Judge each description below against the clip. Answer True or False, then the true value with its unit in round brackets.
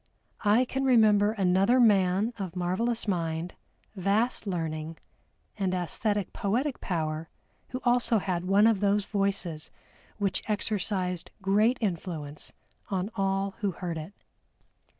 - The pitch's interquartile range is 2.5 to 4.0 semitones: True (3.2 semitones)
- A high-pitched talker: True (195 Hz)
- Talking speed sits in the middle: False (120 wpm)